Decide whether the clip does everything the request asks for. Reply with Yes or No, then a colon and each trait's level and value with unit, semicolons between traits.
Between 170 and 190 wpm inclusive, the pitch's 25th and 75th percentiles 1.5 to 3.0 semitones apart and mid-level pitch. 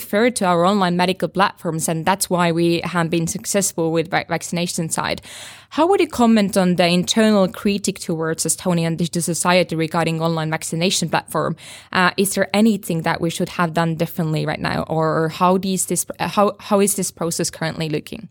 Yes: average, 175 wpm; narrow, 2.5 semitones; medium, 175 Hz